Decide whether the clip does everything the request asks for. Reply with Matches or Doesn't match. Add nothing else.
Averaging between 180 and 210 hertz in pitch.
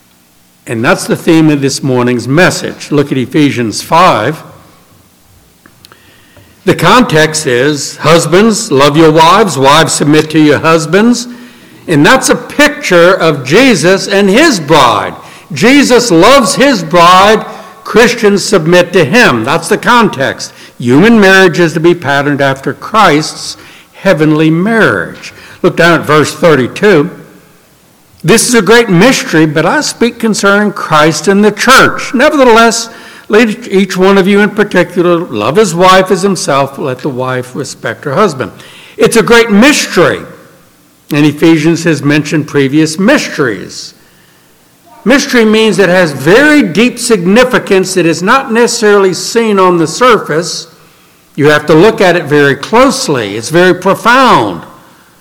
Matches